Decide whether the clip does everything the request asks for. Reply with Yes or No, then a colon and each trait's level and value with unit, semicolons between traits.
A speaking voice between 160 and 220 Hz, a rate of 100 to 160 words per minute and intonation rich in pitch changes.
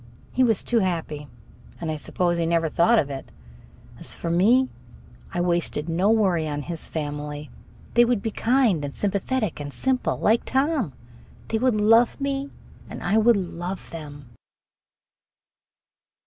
Yes: medium, 185 Hz; average, 150 wpm; wide, 6.6 semitones